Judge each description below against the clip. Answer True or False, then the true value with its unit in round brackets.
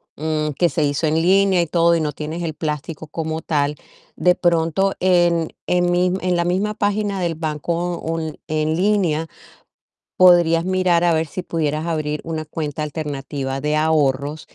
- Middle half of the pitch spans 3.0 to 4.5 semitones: False (2.5 semitones)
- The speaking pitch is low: False (165 Hz)